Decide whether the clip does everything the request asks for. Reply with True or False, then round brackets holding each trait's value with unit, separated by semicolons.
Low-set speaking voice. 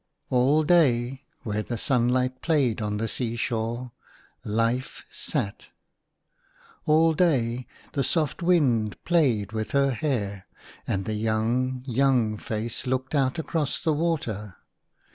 True (125 Hz)